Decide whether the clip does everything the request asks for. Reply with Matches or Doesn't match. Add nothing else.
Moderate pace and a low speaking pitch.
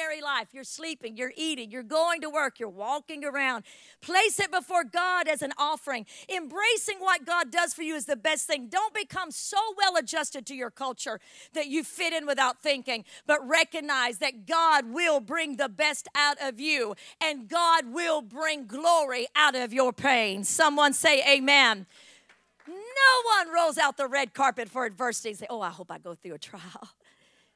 Doesn't match